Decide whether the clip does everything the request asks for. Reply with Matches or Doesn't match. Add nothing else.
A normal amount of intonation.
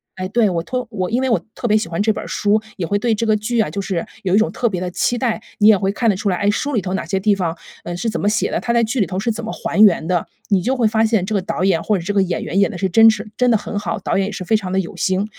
Matches